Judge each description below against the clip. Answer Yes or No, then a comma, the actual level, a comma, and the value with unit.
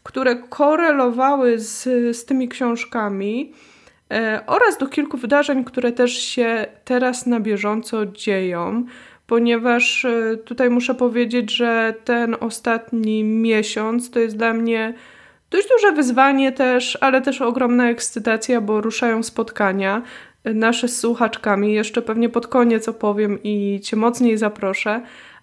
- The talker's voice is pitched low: No, high, 235 Hz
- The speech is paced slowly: No, average, 125 wpm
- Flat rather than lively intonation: Yes, narrow, 2.2 semitones